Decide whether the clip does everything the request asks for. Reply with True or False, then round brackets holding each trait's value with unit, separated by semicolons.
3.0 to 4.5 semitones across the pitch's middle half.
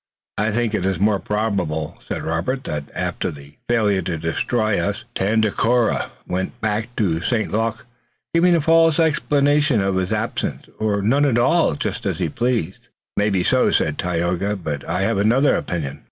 False (4.9 semitones)